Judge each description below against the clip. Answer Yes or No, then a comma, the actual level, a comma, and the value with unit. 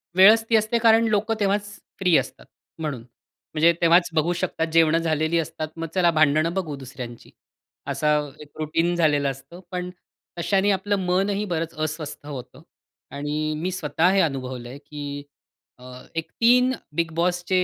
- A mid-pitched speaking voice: Yes, medium, 165 Hz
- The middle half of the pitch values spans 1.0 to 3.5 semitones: No, average, 3.9 semitones